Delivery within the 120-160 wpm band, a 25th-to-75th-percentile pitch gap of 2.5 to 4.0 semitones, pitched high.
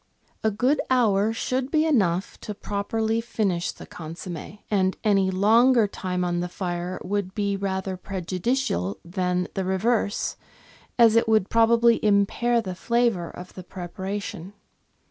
Yes: average, 145 wpm; average, 3.7 semitones; high, 200 Hz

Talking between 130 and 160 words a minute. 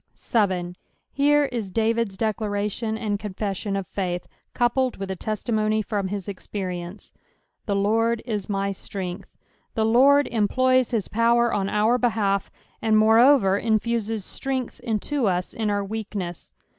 Yes: average, 140 wpm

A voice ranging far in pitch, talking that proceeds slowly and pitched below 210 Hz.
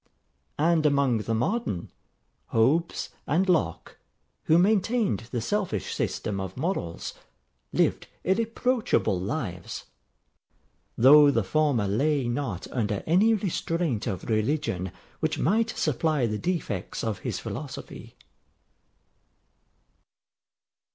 Yes: wide, 8.1 semitones; slow, 100 wpm; medium, 140 Hz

